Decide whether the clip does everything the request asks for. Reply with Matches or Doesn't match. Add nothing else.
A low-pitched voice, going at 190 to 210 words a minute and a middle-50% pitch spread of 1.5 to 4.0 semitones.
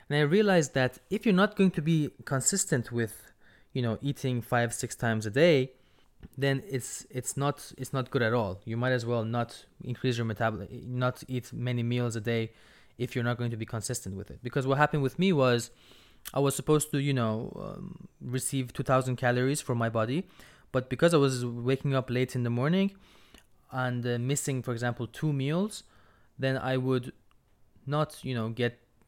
Matches